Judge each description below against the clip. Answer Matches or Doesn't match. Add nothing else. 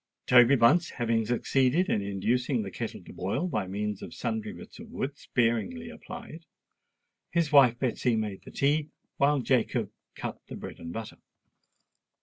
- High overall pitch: Doesn't match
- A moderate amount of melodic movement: Doesn't match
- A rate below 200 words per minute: Matches